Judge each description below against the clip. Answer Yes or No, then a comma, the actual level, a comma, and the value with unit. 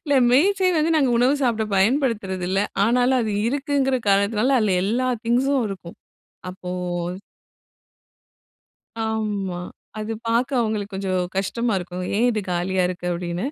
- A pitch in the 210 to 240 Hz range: Yes, high, 220 Hz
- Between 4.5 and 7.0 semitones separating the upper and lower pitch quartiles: Yes, average, 5.1 semitones